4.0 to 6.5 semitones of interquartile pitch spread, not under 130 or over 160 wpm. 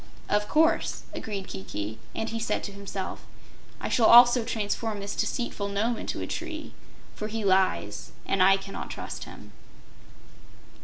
No: average, 3.0 semitones; average, 150 wpm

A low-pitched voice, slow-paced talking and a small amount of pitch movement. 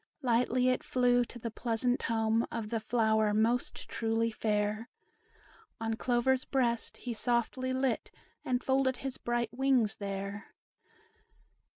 No: high, 235 Hz; slow, 130 wpm; narrow, 2.1 semitones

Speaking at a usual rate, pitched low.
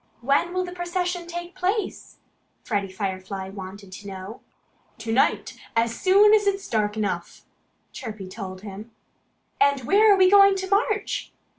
No: average, 150 wpm; very high, 255 Hz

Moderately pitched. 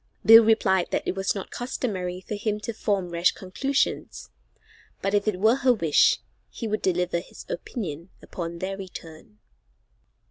No: high, 195 Hz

